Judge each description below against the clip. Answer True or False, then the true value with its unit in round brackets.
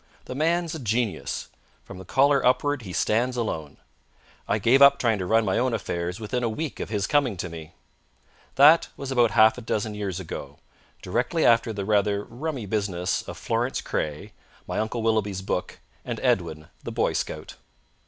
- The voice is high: False (110 Hz)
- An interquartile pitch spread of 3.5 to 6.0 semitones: True (4.6 semitones)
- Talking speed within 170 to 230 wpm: True (180 wpm)